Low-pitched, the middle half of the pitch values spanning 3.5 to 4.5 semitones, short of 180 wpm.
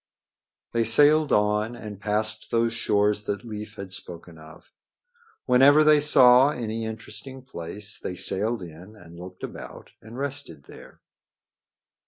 Yes: low, 110 Hz; average, 3.9 semitones; slow, 135 wpm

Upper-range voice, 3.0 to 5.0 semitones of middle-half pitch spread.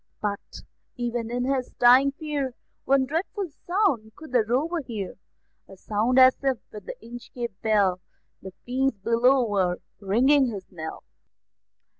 Yes: high, 245 Hz; average, 4.2 semitones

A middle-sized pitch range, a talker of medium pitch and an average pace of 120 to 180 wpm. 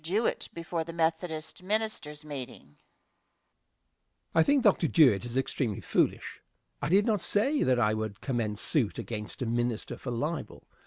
No: wide, 6.3 semitones; medium, 150 Hz; average, 155 wpm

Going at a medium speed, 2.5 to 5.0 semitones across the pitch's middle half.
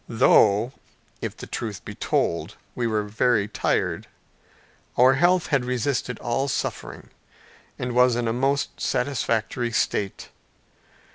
No: slow, 125 wpm; average, 2.8 semitones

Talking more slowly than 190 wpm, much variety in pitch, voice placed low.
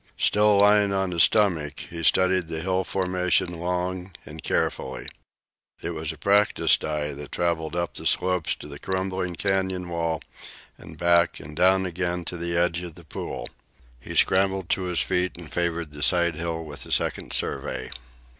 No: average, 175 wpm; narrow, 2.4 semitones; very low, 85 Hz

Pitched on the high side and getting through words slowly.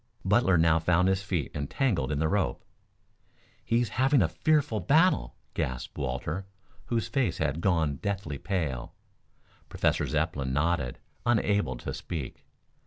No: very low, 85 Hz; slow, 130 wpm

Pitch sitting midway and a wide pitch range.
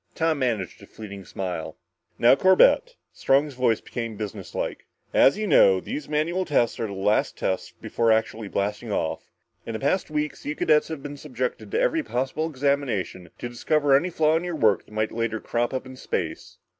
No: low, 130 Hz; wide, 5.8 semitones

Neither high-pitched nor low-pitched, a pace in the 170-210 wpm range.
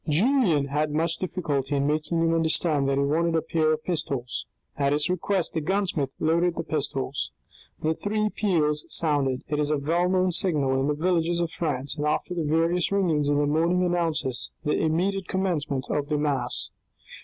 Yes: medium, 155 Hz; average, 180 wpm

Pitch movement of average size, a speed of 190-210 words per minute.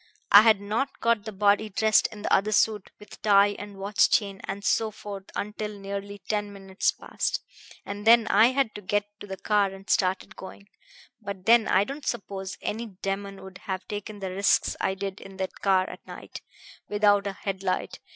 No: narrow, 1.5 semitones; average, 200 wpm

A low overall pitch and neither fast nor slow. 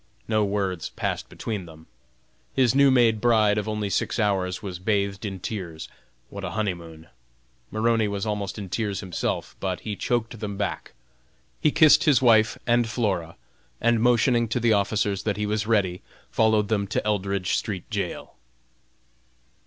Yes: low, 105 Hz; average, 160 wpm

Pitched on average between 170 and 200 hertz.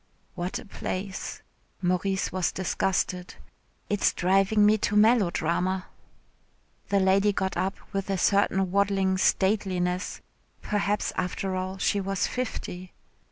Yes: high, 190 Hz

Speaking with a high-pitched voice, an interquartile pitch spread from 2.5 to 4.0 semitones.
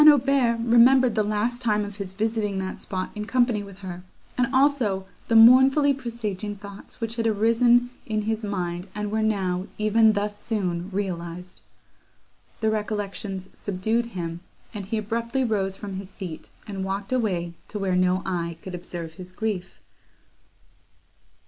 Yes: high, 210 Hz; average, 3.4 semitones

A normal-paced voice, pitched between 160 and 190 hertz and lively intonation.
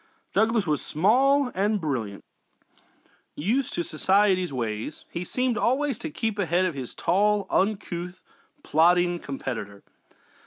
No: slow, 120 wpm; medium, 185 Hz; wide, 6.0 semitones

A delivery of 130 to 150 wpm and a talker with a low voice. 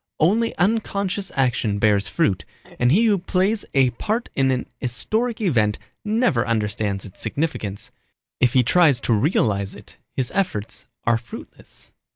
Yes: average, 145 wpm; low, 130 Hz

